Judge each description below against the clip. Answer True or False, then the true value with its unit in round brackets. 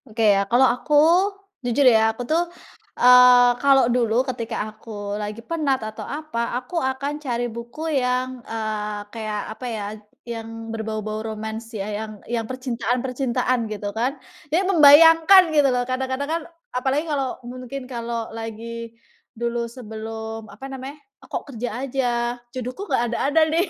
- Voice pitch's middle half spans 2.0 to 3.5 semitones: True (3.0 semitones)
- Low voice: False (245 Hz)